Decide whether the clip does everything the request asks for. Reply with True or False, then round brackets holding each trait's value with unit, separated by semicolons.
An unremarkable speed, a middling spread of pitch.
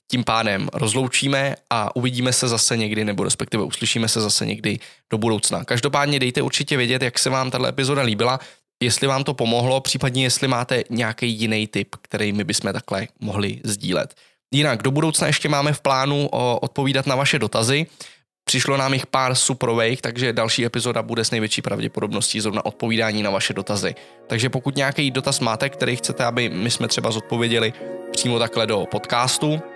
False (175 wpm; 3.1 semitones)